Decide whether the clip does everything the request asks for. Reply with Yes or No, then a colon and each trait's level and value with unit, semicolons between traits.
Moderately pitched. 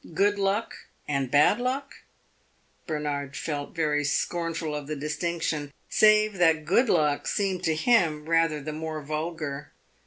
Yes: medium, 160 Hz